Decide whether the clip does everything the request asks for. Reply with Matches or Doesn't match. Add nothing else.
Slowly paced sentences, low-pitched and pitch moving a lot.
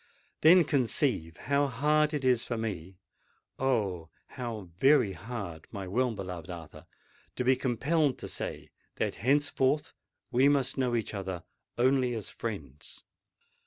Matches